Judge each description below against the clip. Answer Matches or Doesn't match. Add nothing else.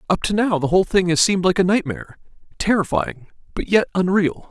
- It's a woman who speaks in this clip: Doesn't match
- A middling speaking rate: Matches